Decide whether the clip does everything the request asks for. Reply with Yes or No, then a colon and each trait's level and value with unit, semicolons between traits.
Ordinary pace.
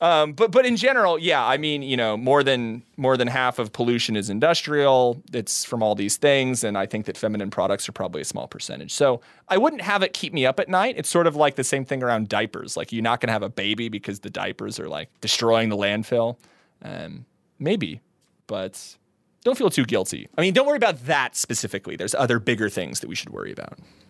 No: fast, 230 wpm